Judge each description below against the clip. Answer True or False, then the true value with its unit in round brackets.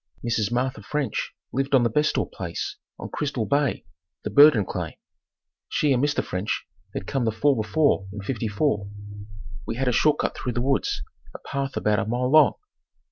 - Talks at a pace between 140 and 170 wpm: False (180 wpm)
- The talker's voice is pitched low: True (125 Hz)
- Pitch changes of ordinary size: True (4.8 semitones)